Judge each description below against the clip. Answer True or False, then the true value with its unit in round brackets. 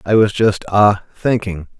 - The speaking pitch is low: True (100 Hz)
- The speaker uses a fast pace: False (100 wpm)